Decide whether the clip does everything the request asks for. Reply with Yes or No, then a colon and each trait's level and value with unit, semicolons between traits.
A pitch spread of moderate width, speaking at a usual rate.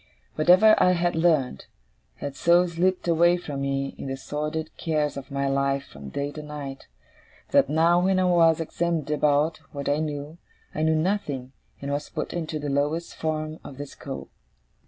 Yes: average, 3.2 semitones; average, 175 wpm